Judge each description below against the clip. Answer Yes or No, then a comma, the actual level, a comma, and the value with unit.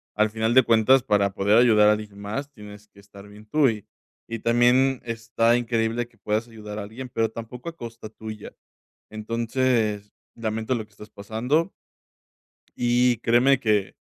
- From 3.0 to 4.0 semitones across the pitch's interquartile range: No, narrow, 2.4 semitones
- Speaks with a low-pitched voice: Yes, low, 115 Hz